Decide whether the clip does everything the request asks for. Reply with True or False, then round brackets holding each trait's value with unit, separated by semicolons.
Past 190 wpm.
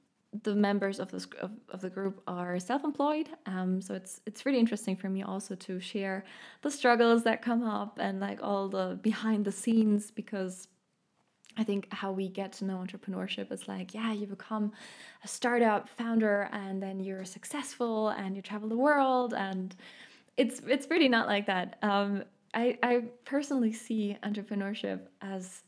False (170 wpm)